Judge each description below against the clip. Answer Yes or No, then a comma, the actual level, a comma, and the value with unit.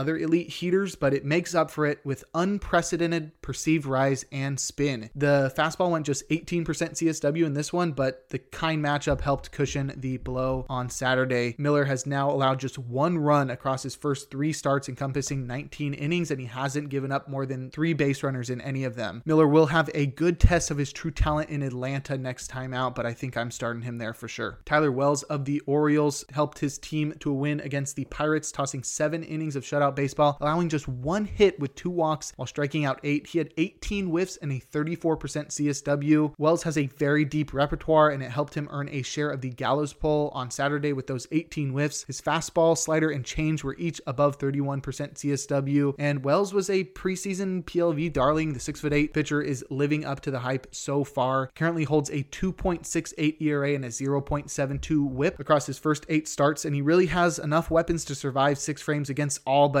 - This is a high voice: No, medium, 145 Hz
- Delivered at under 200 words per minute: No, fast, 205 wpm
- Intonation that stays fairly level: Yes, narrow, 2.3 semitones